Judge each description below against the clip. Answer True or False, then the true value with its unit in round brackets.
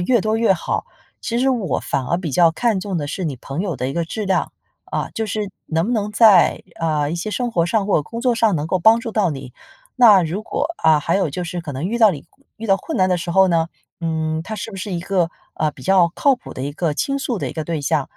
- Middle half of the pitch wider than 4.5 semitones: True (5.1 semitones)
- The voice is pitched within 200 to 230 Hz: False (185 Hz)